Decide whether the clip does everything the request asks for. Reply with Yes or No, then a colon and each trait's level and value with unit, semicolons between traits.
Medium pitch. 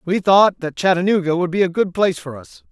Yes: medium, 180 Hz